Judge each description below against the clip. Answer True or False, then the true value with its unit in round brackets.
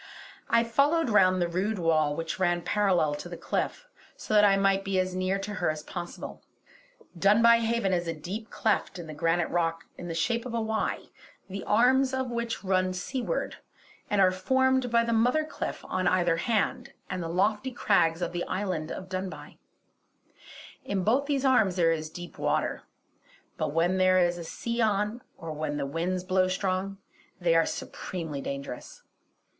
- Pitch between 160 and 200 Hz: True (185 Hz)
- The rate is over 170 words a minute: True (180 wpm)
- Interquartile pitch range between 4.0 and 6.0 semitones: True (4.4 semitones)